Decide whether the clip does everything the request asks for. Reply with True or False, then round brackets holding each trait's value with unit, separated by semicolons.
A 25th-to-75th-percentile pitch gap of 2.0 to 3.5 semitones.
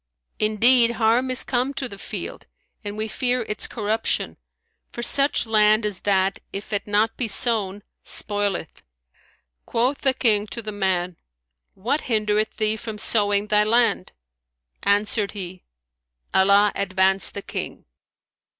True (2.4 semitones)